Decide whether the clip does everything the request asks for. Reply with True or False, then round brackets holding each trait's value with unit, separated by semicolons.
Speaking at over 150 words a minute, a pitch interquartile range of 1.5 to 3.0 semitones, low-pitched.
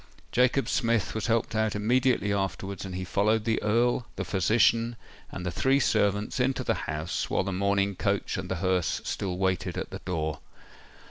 False (180 wpm; 3.7 semitones; 100 Hz)